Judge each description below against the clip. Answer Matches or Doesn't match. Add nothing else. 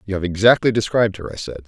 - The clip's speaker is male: Matches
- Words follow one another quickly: Matches